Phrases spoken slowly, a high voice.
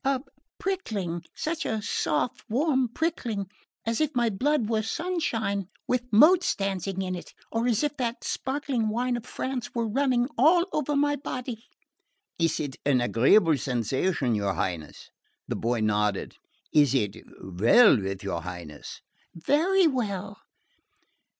Yes: slow, 130 wpm; high, 220 Hz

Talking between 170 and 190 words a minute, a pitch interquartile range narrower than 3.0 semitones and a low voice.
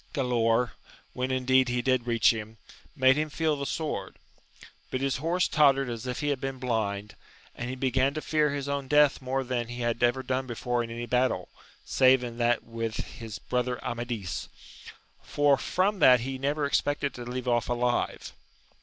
Yes: average, 180 wpm; narrow, 2.5 semitones; low, 125 Hz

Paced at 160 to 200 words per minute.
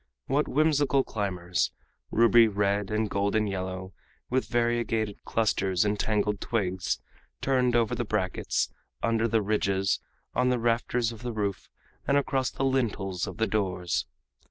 No: average, 140 wpm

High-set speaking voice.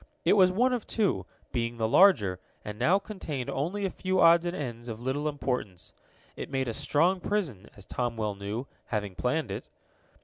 No: low, 135 Hz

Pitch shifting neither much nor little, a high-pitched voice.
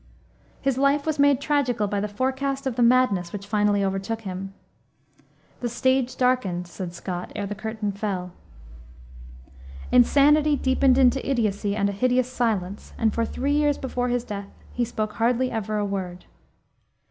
Yes: average, 4.5 semitones; high, 230 Hz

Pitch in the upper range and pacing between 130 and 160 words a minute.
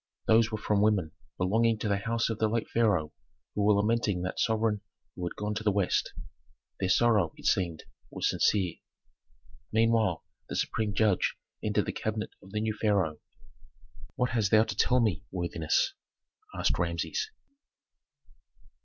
No: low, 105 Hz; average, 155 wpm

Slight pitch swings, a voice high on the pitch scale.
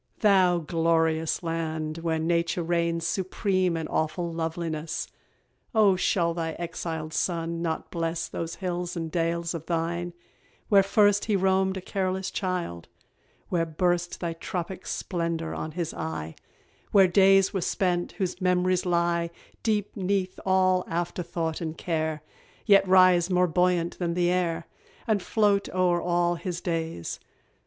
No: narrow, 2.0 semitones; medium, 175 Hz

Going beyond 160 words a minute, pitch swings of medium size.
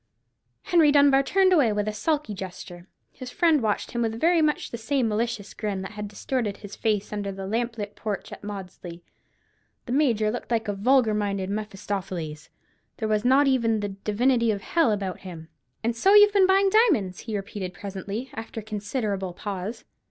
Yes: average, 185 wpm; average, 4.5 semitones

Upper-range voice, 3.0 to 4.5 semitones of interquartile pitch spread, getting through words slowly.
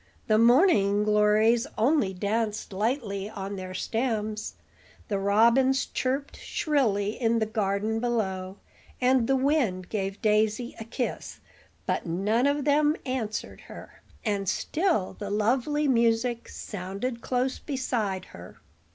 Yes: high, 220 Hz; average, 4.1 semitones; slow, 125 wpm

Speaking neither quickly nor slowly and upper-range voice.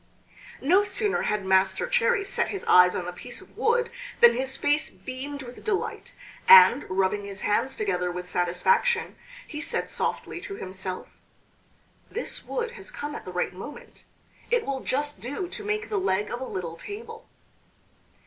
Yes: average, 170 wpm; very high, 270 Hz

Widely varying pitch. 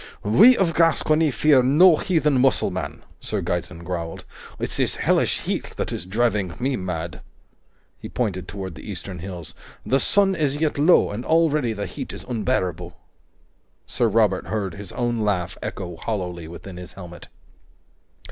Yes: wide, 7.7 semitones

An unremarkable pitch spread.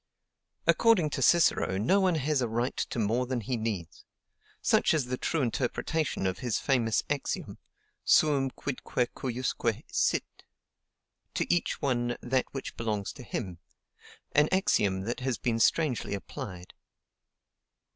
Yes: average, 4.3 semitones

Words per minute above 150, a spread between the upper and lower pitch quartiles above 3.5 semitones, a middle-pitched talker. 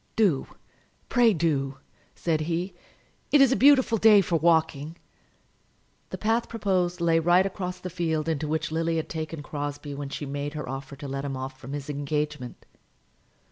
Yes: average, 170 wpm; average, 4.0 semitones; medium, 160 Hz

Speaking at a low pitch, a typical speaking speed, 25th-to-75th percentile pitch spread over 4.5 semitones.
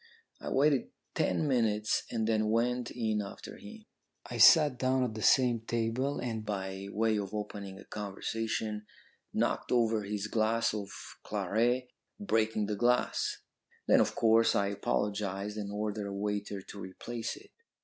No: low, 110 Hz; average, 150 wpm; narrow, 2.6 semitones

